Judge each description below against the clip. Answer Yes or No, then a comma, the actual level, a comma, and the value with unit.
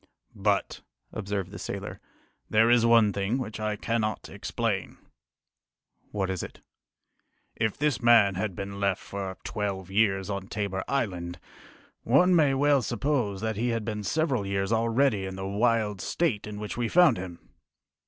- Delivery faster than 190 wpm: No, average, 155 wpm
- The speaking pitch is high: No, low, 105 Hz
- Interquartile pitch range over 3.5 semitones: No, average, 3.2 semitones